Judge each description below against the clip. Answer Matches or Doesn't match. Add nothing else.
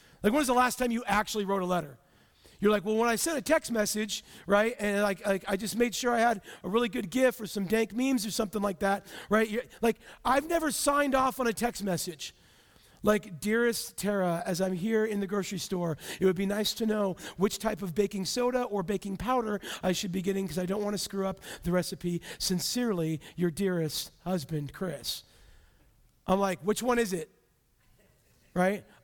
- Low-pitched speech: Doesn't match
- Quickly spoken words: Matches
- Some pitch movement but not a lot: Matches